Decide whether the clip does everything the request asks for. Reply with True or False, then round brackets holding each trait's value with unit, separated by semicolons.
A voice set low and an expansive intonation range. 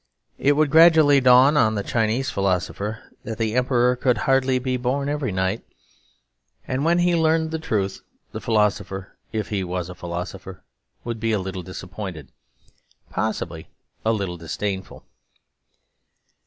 True (110 Hz; 5.8 semitones)